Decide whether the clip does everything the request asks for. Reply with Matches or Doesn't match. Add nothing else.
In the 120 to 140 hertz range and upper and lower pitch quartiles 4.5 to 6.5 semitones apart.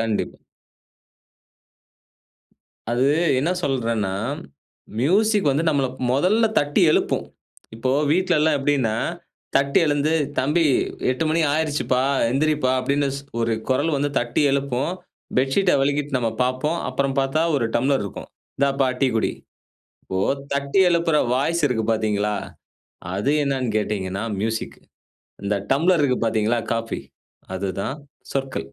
Doesn't match